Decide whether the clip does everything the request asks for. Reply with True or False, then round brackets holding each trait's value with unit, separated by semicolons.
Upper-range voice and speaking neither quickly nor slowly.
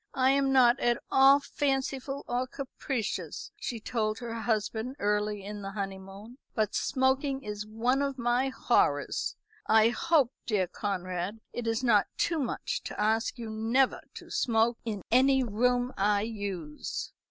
True (230 Hz; 150 wpm)